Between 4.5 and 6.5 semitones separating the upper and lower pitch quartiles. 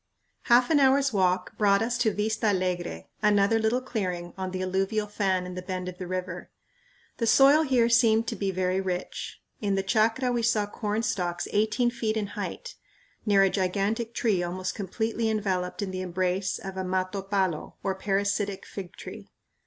No: average, 3.2 semitones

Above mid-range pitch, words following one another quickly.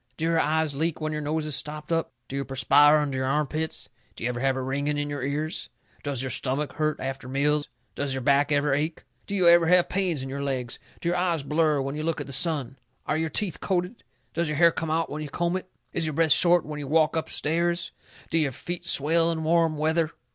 No: medium, 150 Hz; fast, 250 wpm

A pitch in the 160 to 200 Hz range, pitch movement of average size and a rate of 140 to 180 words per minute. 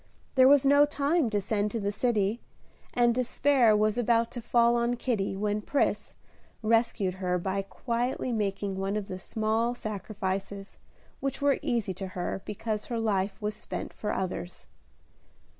No: high, 215 Hz; average, 3.4 semitones; average, 160 wpm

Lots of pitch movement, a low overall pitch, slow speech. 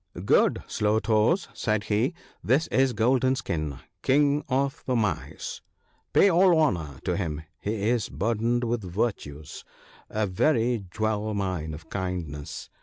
No: wide, 5.9 semitones; low, 110 Hz; average, 155 wpm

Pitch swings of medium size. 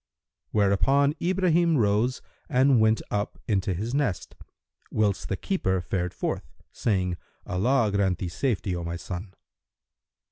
No: wide, 5.8 semitones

